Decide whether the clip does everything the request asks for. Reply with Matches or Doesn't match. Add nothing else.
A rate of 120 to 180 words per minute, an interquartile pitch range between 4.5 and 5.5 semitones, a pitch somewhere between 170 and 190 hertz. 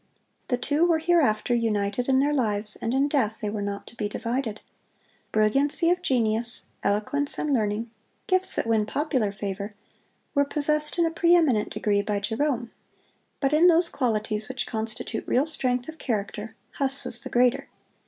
Doesn't match